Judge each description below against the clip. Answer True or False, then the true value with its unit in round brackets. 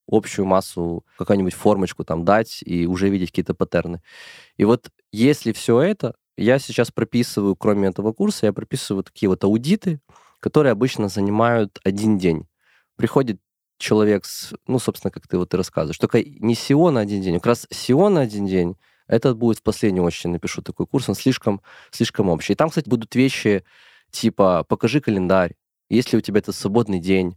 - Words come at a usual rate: False (180 wpm)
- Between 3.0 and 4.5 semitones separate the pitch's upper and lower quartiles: True (4.0 semitones)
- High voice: False (105 Hz)